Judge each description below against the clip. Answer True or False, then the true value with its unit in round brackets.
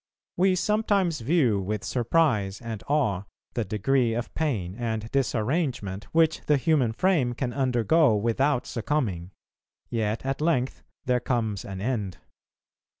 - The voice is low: True (120 Hz)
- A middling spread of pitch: False (5.7 semitones)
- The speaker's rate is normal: False (130 wpm)